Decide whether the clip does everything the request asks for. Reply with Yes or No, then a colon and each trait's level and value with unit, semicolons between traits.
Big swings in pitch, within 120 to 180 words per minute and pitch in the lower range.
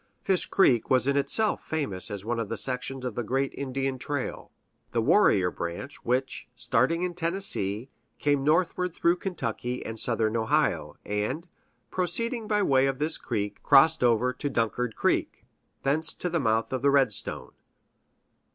Yes: wide, 5.8 semitones; average, 155 wpm; low, 130 Hz